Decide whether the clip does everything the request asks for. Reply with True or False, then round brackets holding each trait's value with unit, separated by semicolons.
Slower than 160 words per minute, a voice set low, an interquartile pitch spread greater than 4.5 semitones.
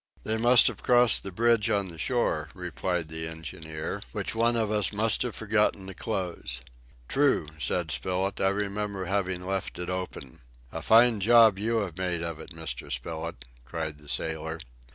False (175 wpm; 95 Hz; 4.9 semitones)